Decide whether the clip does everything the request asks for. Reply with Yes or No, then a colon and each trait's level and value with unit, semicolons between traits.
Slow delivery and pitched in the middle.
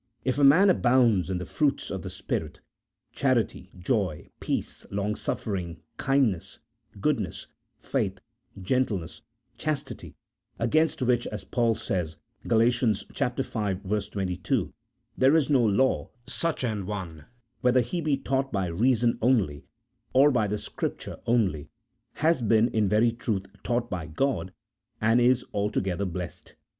No: slow, 130 wpm; low, 115 Hz